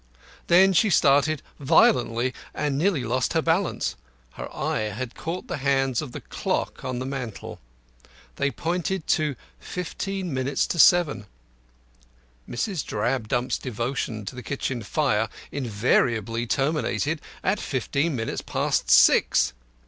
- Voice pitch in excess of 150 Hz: No, low, 135 Hz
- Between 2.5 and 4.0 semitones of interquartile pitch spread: No, average, 5.0 semitones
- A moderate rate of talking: No, slow, 125 wpm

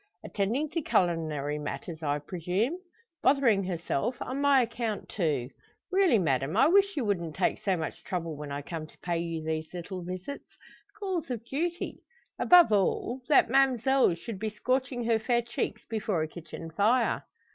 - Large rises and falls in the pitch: Yes, wide, 7.8 semitones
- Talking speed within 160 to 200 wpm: Yes, average, 165 wpm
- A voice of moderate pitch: No, high, 205 Hz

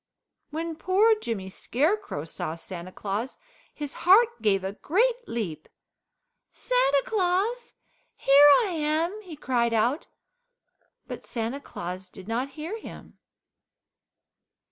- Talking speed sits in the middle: No, slow, 115 wpm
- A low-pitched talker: No, very high, 290 Hz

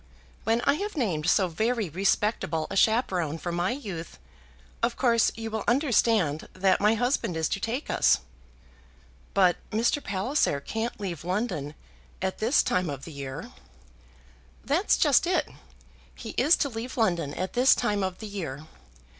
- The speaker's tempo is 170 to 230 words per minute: No, average, 155 wpm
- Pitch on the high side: Yes, high, 200 Hz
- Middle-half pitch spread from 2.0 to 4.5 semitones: No, wide, 5.4 semitones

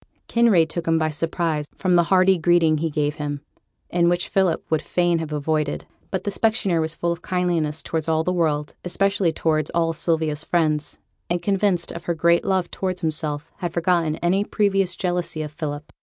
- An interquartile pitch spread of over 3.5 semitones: No, narrow, 2.4 semitones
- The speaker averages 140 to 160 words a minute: No, average, 185 wpm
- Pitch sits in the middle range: Yes, medium, 170 Hz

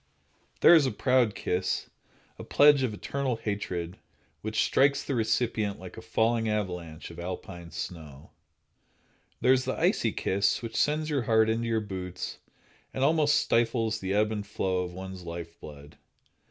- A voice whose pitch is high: No, low, 110 Hz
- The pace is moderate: Yes, average, 160 wpm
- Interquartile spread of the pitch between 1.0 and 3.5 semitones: No, average, 5.2 semitones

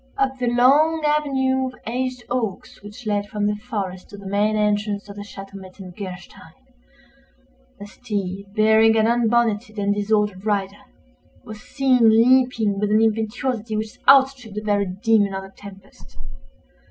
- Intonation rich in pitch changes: No, average, 3.2 semitones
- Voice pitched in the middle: No, high, 215 Hz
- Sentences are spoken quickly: No, average, 150 wpm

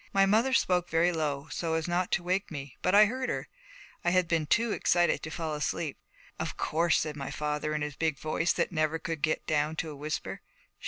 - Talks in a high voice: No, medium, 160 Hz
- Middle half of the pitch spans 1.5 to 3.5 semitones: Yes, average, 2.8 semitones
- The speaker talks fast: Yes, fast, 220 wpm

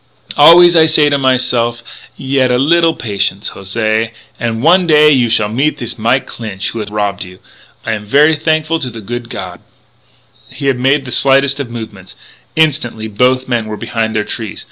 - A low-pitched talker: Yes, low, 120 Hz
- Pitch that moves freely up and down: No, average, 4.7 semitones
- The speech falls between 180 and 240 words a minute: Yes, average, 185 wpm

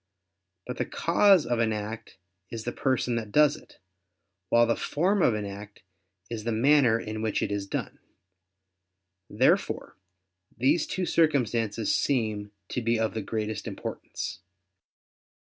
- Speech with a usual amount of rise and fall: Yes, average, 4.2 semitones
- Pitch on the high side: No, low, 115 Hz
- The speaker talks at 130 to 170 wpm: Yes, average, 145 wpm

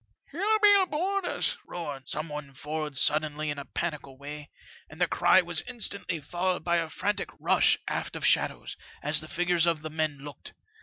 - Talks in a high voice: No, medium, 160 Hz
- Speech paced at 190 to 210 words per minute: Yes, average, 200 wpm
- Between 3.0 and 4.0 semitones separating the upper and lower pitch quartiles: Yes, average, 3.7 semitones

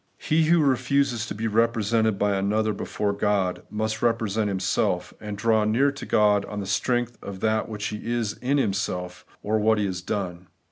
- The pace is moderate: Yes, average, 180 wpm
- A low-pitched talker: Yes, low, 110 Hz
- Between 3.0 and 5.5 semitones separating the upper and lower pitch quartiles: No, narrow, 2.5 semitones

